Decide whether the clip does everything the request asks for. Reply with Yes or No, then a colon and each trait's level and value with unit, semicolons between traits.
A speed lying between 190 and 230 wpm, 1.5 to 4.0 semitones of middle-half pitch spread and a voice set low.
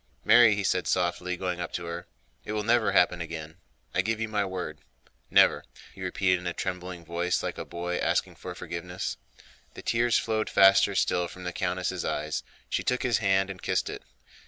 Yes: average, 195 wpm; average, 2.9 semitones; very low, 90 Hz